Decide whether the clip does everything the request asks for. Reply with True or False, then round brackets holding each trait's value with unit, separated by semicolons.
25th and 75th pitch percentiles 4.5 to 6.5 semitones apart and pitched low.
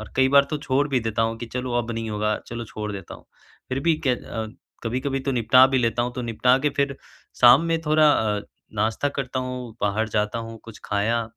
False (3.0 semitones; 120 Hz)